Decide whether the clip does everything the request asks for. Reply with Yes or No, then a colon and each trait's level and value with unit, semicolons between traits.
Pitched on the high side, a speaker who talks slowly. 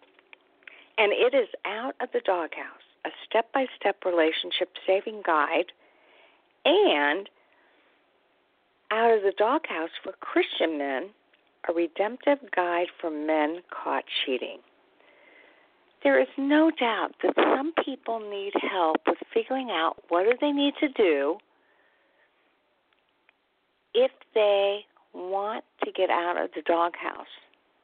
Yes: high, 220 Hz; slow, 120 wpm